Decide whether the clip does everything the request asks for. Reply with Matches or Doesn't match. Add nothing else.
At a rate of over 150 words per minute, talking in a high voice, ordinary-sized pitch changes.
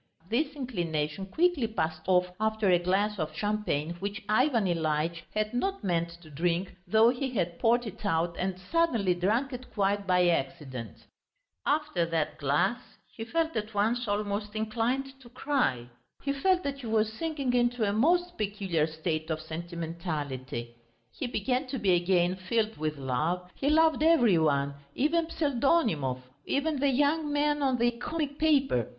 Doesn't match